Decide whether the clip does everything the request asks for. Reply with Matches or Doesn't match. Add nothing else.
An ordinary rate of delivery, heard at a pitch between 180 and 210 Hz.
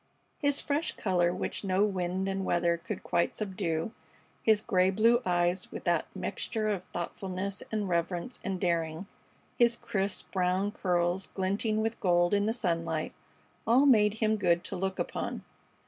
Matches